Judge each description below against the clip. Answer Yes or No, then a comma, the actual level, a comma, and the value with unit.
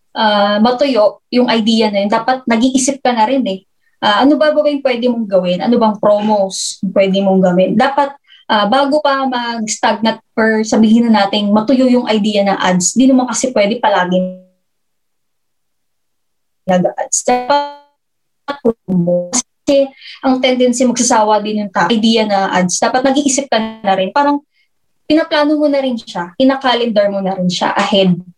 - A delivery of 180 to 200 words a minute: No, average, 155 wpm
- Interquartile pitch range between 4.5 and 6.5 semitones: Yes, average, 4.9 semitones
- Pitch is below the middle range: No, high, 230 Hz